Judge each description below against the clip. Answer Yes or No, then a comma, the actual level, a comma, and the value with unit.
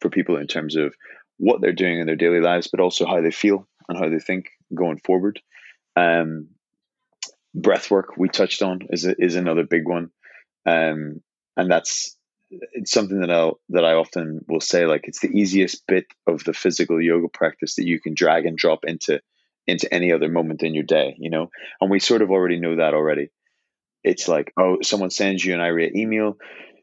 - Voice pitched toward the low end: Yes, very low, 85 Hz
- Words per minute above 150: Yes, average, 200 wpm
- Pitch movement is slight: Yes, narrow, 2.2 semitones